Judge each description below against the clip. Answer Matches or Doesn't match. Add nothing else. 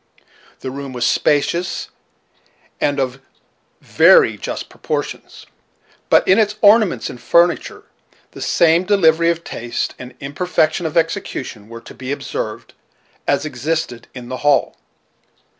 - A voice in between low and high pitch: Matches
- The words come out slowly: Matches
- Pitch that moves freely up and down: Doesn't match